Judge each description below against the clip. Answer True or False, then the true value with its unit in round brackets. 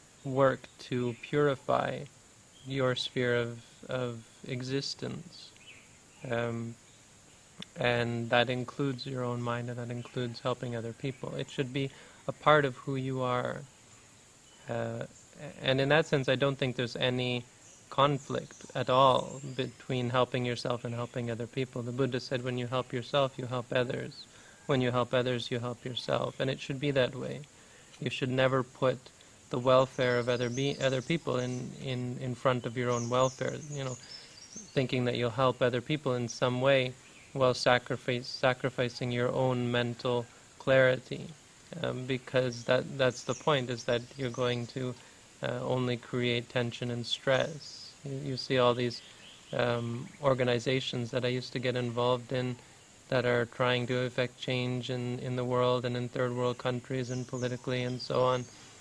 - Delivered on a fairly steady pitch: True (1.3 semitones)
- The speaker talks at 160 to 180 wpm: True (165 wpm)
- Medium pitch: False (125 Hz)